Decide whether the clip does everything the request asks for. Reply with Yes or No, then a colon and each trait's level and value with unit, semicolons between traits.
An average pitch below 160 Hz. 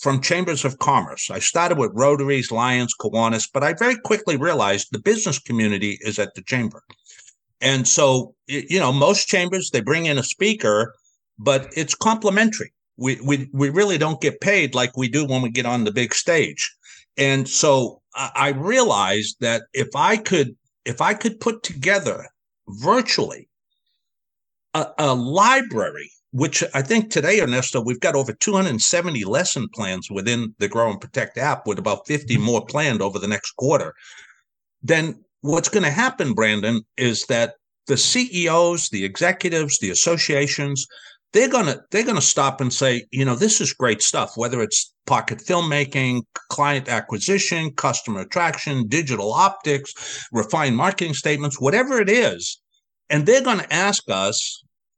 Yes: medium, 140 Hz